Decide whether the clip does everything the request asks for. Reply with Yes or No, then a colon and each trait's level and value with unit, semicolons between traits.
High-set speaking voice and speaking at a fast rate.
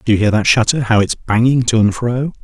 No: low, 115 Hz; fast, 270 wpm